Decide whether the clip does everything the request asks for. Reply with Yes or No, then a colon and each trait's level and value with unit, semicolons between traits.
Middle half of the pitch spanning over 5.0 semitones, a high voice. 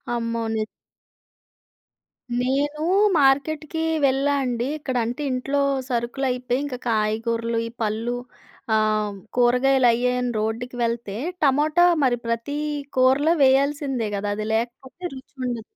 No: average, 2.8 semitones; very high, 250 Hz